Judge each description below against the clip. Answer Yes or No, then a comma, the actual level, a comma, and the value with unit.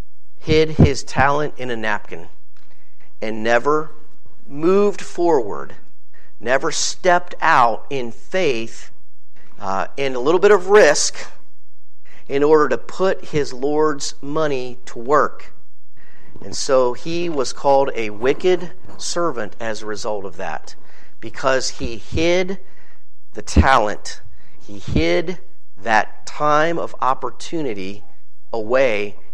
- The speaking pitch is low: No, medium, 145 Hz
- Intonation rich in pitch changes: Yes, wide, 7.1 semitones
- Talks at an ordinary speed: No, slow, 115 wpm